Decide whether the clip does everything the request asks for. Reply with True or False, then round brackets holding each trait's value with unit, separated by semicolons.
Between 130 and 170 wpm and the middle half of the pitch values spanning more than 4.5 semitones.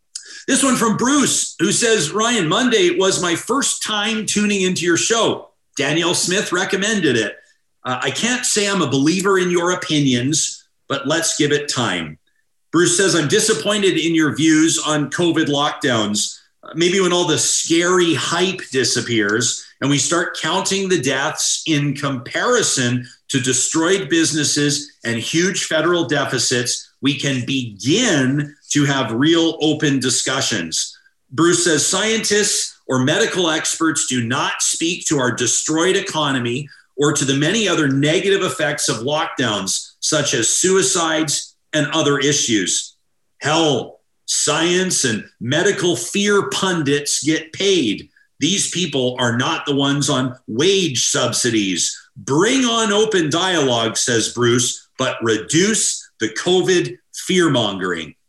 True (135 wpm; 5.1 semitones)